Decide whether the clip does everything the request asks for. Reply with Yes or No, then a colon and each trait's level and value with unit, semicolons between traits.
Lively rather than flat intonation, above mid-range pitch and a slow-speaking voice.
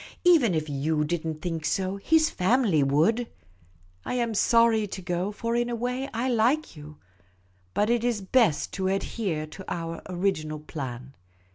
No: wide, 6.9 semitones; high, 195 Hz; average, 165 wpm